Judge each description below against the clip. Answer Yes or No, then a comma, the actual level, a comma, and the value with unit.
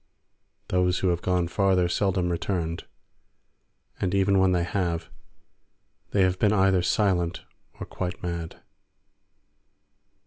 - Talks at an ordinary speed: No, slow, 115 wpm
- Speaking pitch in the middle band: No, very low, 90 Hz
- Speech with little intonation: Yes, narrow, 1.8 semitones